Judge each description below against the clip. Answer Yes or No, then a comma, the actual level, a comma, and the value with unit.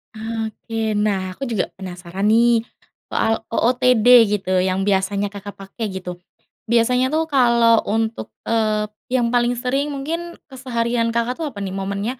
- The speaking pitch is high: Yes, high, 225 Hz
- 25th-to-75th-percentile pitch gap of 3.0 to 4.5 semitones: Yes, average, 3.5 semitones